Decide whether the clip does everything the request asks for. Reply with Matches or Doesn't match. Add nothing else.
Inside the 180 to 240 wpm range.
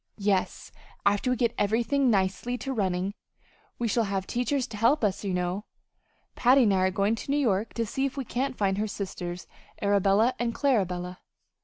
Matches